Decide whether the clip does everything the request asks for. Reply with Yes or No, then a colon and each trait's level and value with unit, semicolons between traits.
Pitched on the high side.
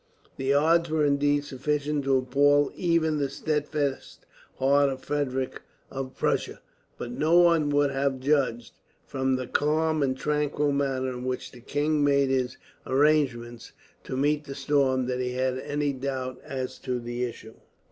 No: medium, 140 Hz